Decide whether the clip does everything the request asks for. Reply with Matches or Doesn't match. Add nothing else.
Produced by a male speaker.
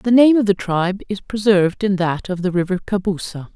Doesn't match